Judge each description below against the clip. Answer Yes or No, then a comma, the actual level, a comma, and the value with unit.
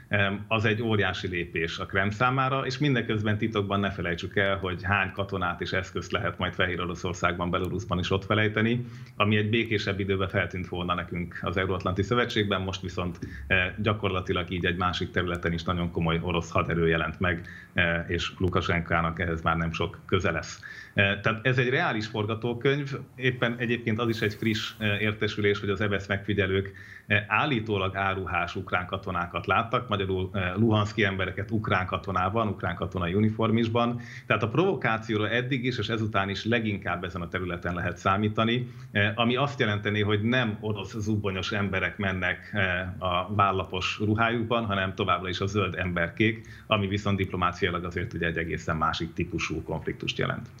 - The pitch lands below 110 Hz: Yes, low, 100 Hz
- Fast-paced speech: Yes, fast, 160 wpm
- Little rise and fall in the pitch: No, average, 3.4 semitones